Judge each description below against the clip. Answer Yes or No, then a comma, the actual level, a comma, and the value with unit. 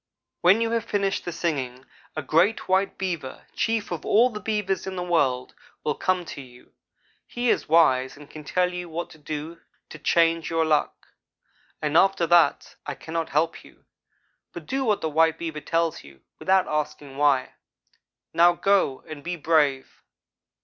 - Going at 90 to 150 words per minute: No, average, 170 wpm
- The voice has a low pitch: No, medium, 165 Hz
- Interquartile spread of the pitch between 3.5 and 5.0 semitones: Yes, average, 3.9 semitones